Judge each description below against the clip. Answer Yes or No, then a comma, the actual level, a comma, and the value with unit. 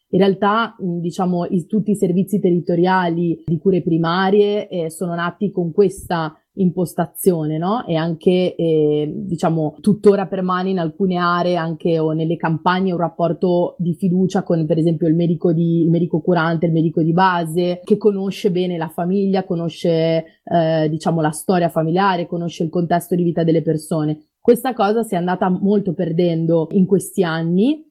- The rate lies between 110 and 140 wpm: No, average, 165 wpm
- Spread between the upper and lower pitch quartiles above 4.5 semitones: No, narrow, 2.5 semitones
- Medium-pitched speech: Yes, medium, 175 Hz